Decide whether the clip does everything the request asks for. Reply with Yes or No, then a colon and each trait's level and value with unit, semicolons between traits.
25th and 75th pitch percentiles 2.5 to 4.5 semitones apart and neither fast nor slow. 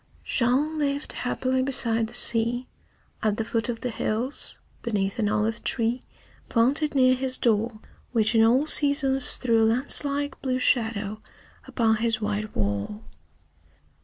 Yes: average, 2.9 semitones; average, 145 wpm